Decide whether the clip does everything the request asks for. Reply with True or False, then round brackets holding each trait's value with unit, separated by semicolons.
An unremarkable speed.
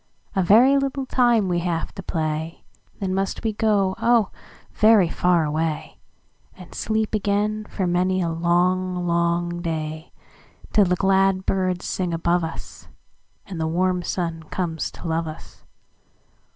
False (130 wpm)